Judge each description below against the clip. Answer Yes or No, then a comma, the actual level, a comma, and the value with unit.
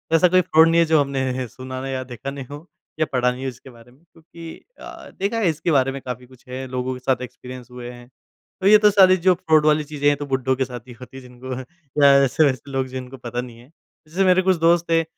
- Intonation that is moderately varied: Yes, average, 4.3 semitones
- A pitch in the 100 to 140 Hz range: Yes, low, 135 Hz